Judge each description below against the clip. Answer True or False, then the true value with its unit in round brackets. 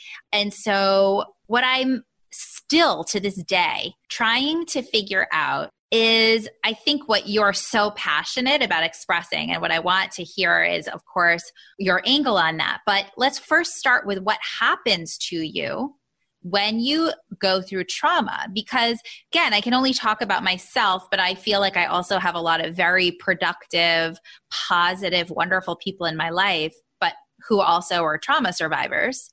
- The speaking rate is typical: True (165 wpm)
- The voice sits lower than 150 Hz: False (200 Hz)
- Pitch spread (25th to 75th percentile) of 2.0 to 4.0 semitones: False (5.1 semitones)